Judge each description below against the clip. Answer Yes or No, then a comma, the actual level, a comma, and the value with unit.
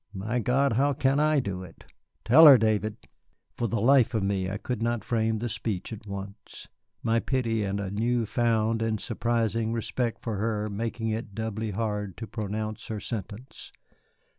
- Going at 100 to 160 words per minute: No, average, 175 wpm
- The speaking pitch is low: Yes, low, 110 Hz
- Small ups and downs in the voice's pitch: Yes, narrow, 2.2 semitones